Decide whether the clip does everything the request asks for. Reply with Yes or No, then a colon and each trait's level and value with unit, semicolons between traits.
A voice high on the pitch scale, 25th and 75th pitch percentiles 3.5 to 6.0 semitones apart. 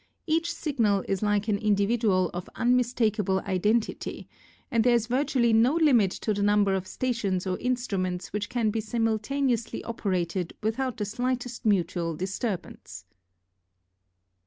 Yes: high, 215 Hz; average, 3.8 semitones